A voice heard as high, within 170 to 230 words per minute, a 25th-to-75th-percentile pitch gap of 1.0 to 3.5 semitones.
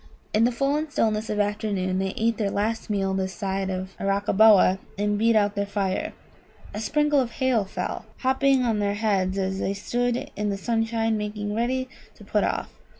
Yes: high, 210 Hz; average, 190 wpm; average, 2.8 semitones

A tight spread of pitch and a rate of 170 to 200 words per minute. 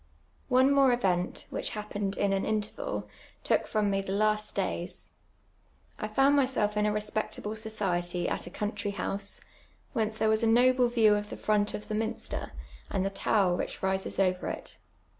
Yes: narrow, 2.0 semitones; average, 175 wpm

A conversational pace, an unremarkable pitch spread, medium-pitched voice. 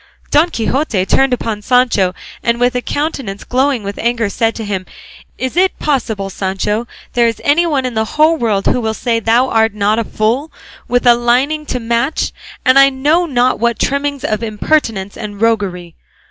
No: average, 180 wpm; average, 3.9 semitones; high, 235 Hz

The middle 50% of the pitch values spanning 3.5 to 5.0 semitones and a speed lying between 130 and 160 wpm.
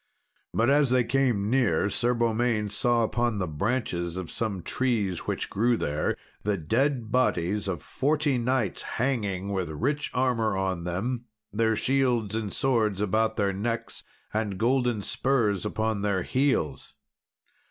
Yes: average, 3.9 semitones; average, 140 wpm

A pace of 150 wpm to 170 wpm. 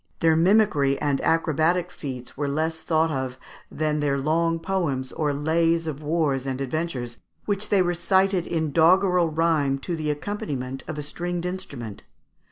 Yes: average, 155 wpm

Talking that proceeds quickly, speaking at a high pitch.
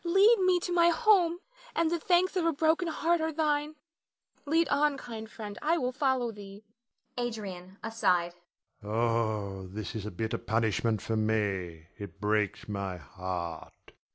No: average, 155 wpm; high, 210 Hz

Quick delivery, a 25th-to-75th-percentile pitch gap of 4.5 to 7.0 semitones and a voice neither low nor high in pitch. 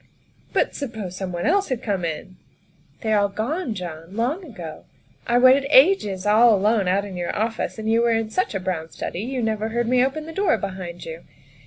No: fast, 215 wpm; average, 5.1 semitones; high, 220 Hz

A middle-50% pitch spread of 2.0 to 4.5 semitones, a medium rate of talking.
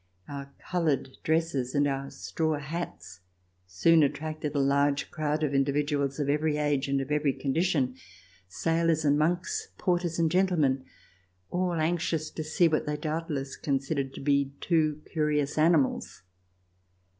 Yes: narrow, 2.6 semitones; average, 145 wpm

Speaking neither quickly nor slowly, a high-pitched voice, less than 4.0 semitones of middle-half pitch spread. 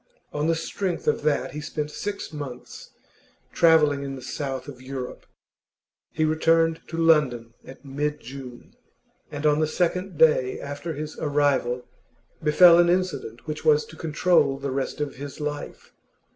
No: average, 155 wpm; medium, 150 Hz; average, 2.8 semitones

